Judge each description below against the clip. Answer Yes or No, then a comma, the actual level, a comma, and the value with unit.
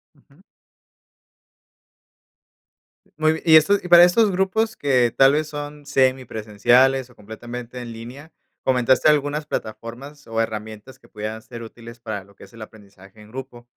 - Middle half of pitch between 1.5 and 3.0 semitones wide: No, average, 4.6 semitones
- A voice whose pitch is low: Yes, low, 125 Hz